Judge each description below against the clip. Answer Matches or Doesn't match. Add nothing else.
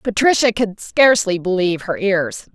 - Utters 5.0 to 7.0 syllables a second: Doesn't match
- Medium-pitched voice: Doesn't match